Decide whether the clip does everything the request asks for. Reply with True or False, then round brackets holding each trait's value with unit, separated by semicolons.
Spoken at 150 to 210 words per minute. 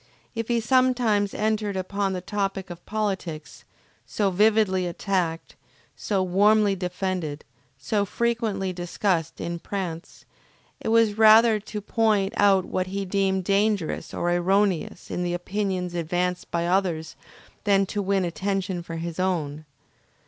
False (135 wpm)